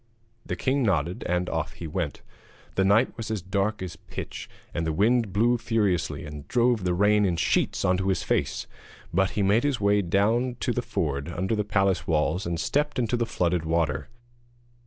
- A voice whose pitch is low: Yes, very low, 95 Hz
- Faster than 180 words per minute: Yes, average, 190 wpm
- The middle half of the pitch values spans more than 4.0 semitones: Yes, average, 4.6 semitones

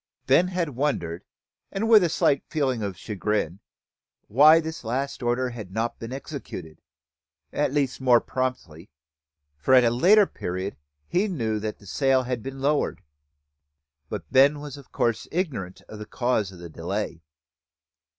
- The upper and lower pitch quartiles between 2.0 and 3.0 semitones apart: No, average, 5.2 semitones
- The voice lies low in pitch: Yes, low, 125 Hz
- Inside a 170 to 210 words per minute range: No, average, 150 wpm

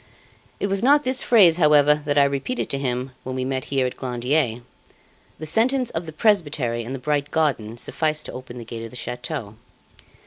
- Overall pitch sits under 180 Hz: Yes, medium, 140 Hz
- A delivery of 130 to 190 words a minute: No, average, 200 wpm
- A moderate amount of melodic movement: Yes, average, 4.4 semitones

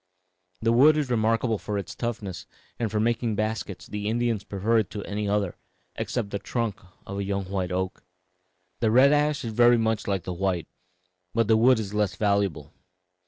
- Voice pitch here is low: Yes, low, 105 Hz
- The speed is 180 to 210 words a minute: Yes, average, 185 wpm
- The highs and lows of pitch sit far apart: No, average, 2.9 semitones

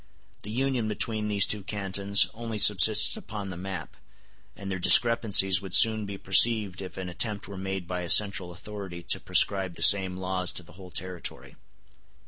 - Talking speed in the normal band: Yes, average, 175 wpm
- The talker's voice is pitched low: Yes, very low, 95 Hz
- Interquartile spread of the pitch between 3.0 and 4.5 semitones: No, narrow, 2.4 semitones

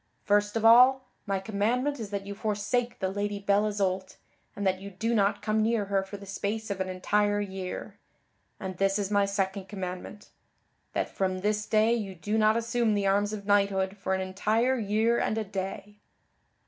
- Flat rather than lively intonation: Yes, narrow, 1.9 semitones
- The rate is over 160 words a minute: Yes, average, 190 wpm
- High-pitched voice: Yes, high, 205 Hz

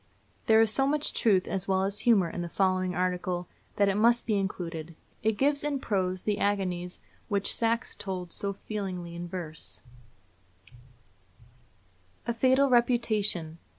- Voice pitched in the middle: No, high, 195 Hz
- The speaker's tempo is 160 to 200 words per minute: No, average, 150 wpm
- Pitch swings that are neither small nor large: Yes, average, 3.9 semitones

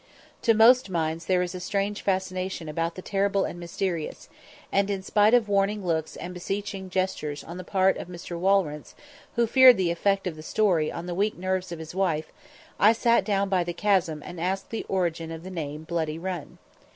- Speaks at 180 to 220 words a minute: Yes, average, 200 wpm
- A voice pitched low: No, medium, 185 Hz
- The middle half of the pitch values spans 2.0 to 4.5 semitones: Yes, average, 2.9 semitones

